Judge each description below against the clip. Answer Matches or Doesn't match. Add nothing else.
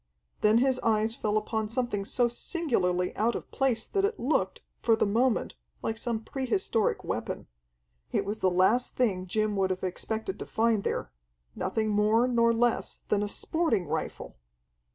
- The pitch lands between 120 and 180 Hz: Doesn't match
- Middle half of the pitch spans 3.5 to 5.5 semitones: Doesn't match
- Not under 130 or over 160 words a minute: Doesn't match